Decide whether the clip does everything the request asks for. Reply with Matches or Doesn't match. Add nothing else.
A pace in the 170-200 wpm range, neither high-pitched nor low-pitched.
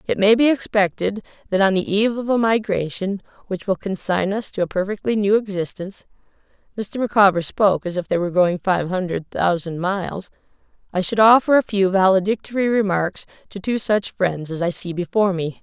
Doesn't match